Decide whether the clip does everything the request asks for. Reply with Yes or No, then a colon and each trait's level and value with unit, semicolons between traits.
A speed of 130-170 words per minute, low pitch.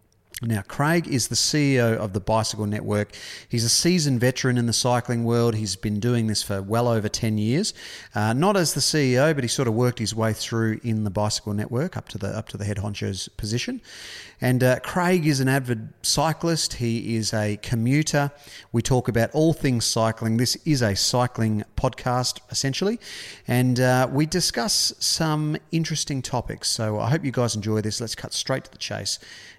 No: average, 195 wpm; low, 120 Hz